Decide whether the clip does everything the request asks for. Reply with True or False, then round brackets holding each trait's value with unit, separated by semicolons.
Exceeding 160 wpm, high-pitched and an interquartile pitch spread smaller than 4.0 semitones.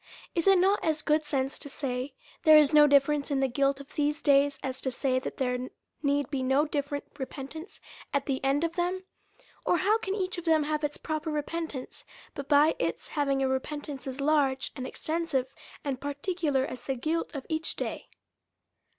True (195 wpm; 285 Hz; 2.6 semitones)